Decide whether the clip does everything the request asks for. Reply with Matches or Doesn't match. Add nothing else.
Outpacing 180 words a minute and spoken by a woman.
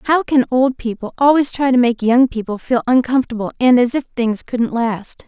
Matches